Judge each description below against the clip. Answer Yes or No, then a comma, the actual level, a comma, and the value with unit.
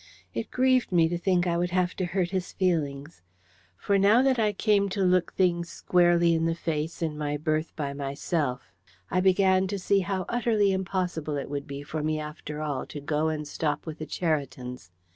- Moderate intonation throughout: Yes, average, 3.8 semitones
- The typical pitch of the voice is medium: Yes, medium, 170 Hz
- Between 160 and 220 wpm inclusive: Yes, average, 200 wpm